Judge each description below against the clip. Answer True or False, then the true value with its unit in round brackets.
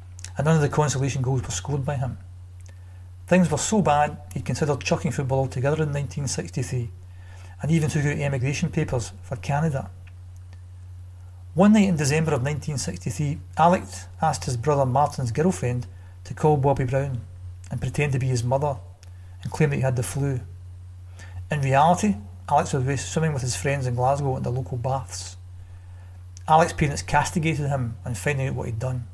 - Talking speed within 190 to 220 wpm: False (170 wpm)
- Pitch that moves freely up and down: True (8.1 semitones)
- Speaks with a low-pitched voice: True (130 Hz)